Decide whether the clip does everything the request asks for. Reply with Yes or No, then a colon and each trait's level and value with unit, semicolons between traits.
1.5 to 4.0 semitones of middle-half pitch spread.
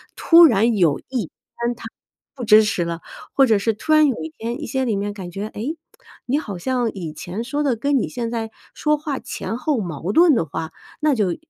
No: wide, 5.6 semitones